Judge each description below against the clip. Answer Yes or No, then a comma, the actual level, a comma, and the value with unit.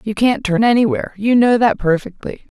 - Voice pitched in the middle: No, high, 220 Hz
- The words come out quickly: No, average, 185 wpm